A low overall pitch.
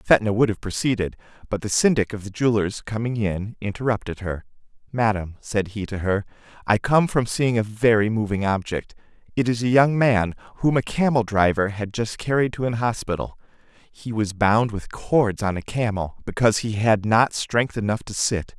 Yes: low, 110 Hz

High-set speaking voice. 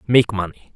No: low, 105 Hz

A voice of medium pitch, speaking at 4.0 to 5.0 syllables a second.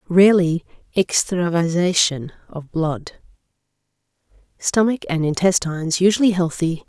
Yes: medium, 170 Hz; 4.5 syllables/s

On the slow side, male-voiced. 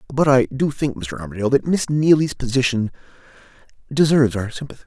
No: average, 160 wpm; male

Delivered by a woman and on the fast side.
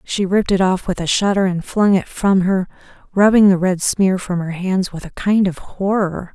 Yes: female; fast, 225 wpm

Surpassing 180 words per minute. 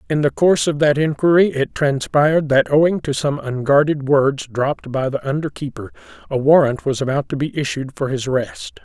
Yes: average, 195 wpm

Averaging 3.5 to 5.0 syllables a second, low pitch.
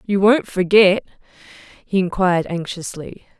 No: 4.5 syllables/s; high, 190 Hz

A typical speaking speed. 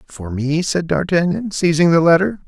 Yes: average, 170 wpm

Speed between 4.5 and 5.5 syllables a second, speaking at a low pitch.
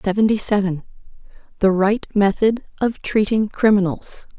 No: 4.6 syllables/s; high, 205 Hz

